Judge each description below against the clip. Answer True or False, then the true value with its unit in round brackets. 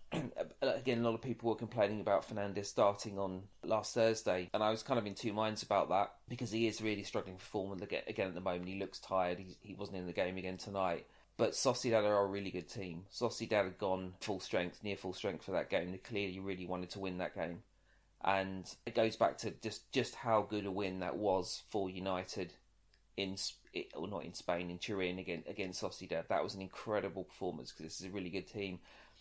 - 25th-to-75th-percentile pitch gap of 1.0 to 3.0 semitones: True (2.5 semitones)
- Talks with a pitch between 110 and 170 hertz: False (95 Hz)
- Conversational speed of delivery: False (220 wpm)